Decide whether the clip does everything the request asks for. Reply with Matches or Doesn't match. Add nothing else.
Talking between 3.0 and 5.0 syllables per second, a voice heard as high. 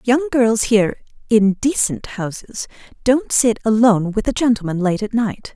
Matches